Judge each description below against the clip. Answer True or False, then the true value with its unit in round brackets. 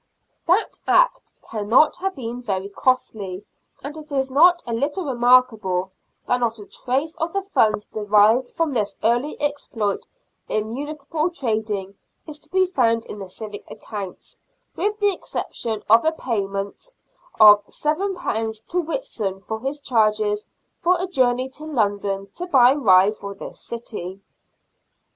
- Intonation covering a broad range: True (6.4 semitones)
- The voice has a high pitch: True (240 Hz)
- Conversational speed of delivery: True (145 wpm)